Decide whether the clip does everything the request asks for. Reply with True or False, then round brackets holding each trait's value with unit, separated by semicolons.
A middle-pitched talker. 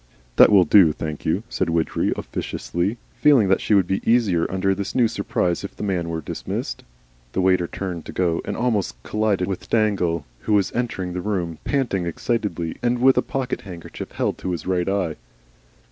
False (95 Hz)